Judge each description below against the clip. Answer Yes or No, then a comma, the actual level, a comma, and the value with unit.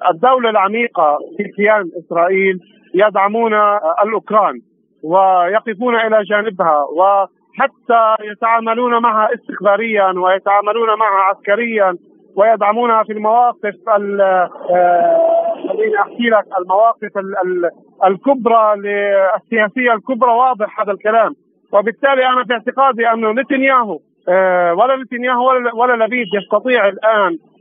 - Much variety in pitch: No, average, 3.6 semitones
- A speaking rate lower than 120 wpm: Yes, average, 90 wpm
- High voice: Yes, high, 215 Hz